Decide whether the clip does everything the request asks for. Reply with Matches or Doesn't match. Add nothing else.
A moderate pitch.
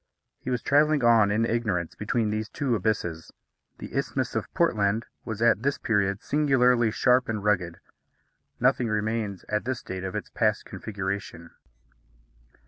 Doesn't match